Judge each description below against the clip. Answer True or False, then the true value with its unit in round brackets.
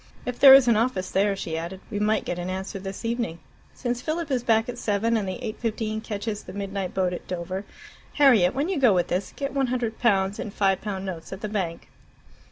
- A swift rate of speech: True (225 wpm)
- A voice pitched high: True (210 Hz)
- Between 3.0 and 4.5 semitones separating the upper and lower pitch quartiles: True (3.9 semitones)